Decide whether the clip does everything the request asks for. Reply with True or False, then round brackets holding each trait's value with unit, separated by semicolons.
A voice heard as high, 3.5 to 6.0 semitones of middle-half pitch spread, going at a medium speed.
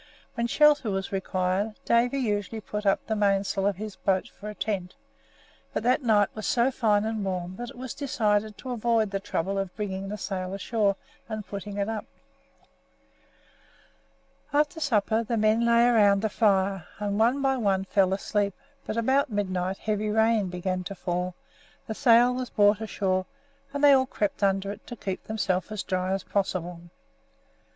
False (210 Hz; 2.9 semitones; 175 wpm)